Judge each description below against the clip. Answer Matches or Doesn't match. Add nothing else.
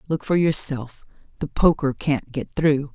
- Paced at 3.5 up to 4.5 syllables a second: Matches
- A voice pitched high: Doesn't match